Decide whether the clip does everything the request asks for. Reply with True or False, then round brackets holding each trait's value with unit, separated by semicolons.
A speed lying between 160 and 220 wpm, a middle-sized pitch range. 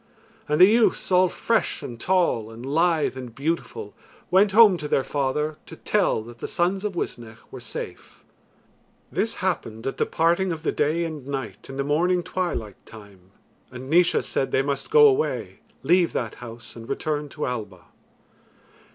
False (170 wpm; 6.7 semitones)